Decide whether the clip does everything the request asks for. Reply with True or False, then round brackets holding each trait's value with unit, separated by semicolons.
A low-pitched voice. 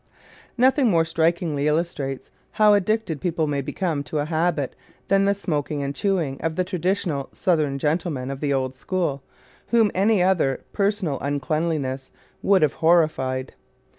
False (160 Hz)